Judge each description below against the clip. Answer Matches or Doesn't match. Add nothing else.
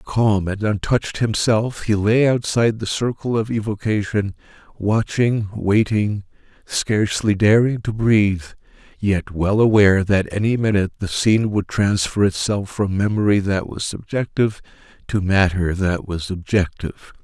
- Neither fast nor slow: Doesn't match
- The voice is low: Matches